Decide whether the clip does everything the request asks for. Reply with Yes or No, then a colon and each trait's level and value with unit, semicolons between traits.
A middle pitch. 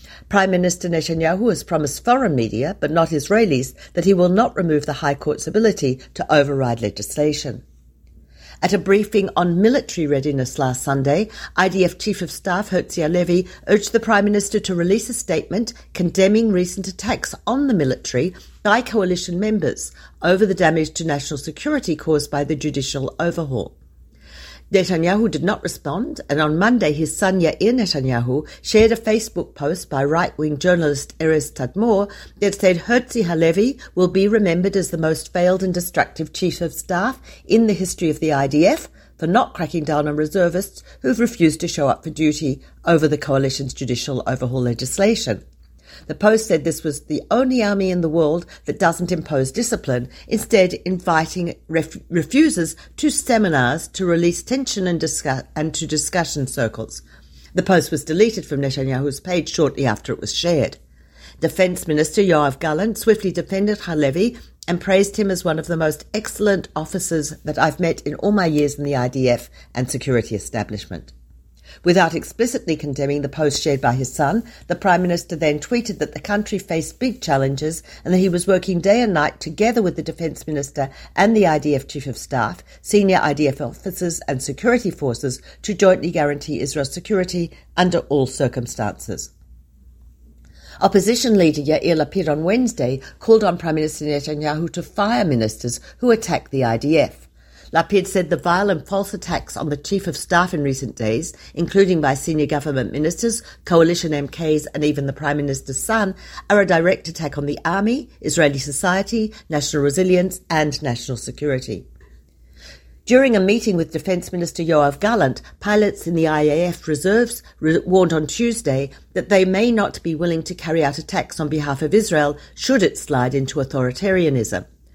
Yes: medium, 160 Hz